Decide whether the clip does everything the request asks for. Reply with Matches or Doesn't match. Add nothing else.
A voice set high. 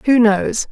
Matches